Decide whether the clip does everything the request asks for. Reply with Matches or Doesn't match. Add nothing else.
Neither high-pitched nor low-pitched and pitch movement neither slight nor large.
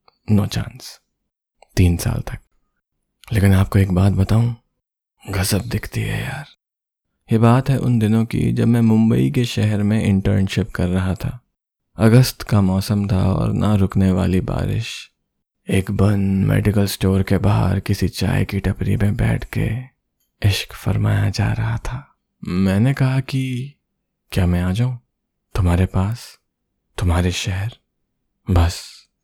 Doesn't match